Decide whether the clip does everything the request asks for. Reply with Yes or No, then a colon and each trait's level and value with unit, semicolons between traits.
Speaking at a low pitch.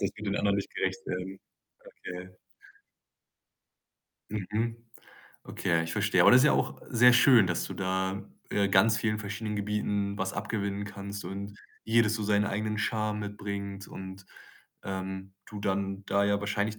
Yes: low, 100 Hz